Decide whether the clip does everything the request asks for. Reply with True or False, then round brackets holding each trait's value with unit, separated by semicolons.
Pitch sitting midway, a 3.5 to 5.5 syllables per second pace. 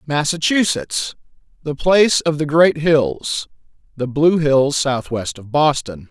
False (150 Hz; 2.8 syllables/s)